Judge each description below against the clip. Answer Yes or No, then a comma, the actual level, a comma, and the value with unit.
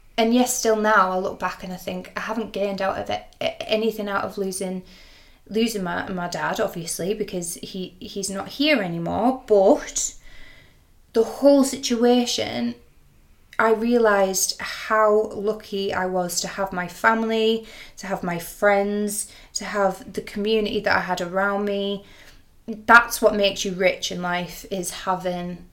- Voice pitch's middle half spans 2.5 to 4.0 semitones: Yes, average, 3.1 semitones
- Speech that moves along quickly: No, average, 155 wpm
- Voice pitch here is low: No, high, 200 Hz